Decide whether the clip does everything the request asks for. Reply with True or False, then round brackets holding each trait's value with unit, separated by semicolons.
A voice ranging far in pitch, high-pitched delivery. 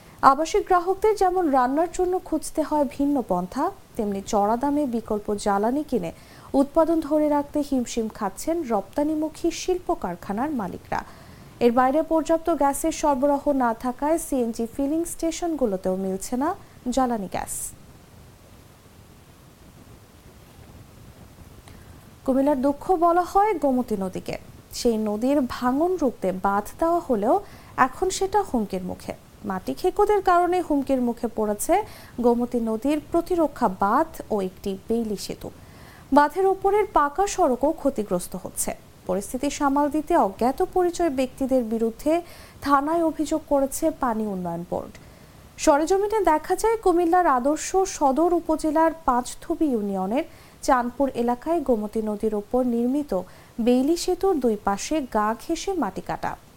True (5.9 semitones; 285 Hz)